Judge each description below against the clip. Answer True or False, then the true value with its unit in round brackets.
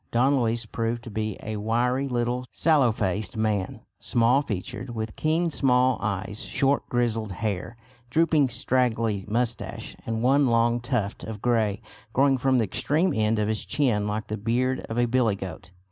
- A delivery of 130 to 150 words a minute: False (160 wpm)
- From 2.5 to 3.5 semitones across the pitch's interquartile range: True (2.8 semitones)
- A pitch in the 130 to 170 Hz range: False (115 Hz)